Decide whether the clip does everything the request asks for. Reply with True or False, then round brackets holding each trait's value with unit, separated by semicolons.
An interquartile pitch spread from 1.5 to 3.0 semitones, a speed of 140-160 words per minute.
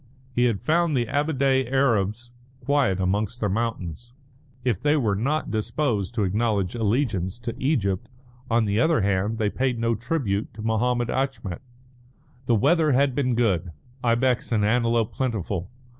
False (4.3 semitones; 150 wpm)